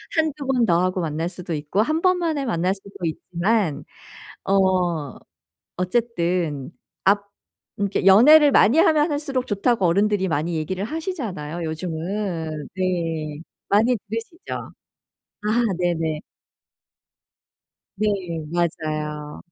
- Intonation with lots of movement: Yes, wide, 6.0 semitones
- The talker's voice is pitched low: No, high, 190 Hz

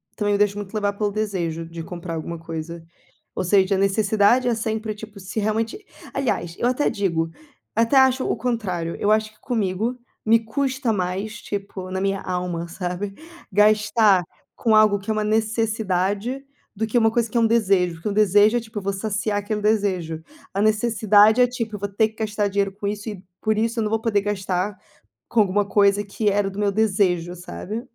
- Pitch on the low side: No, high, 205 Hz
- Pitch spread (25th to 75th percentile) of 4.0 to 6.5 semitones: No, narrow, 2.4 semitones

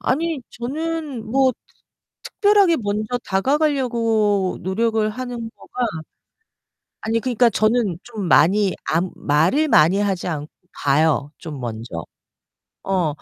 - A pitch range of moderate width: No, wide, 6.4 semitones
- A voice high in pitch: Yes, high, 215 Hz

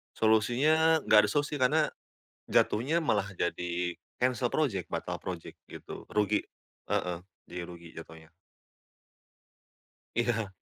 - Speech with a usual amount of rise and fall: No, wide, 7.4 semitones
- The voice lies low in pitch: Yes, low, 110 Hz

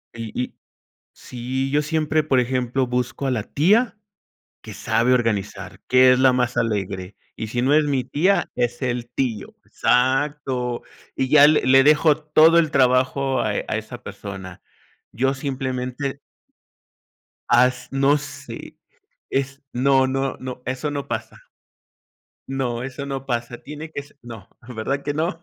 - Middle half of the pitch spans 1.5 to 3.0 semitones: Yes, narrow, 2.6 semitones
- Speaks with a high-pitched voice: No, low, 130 Hz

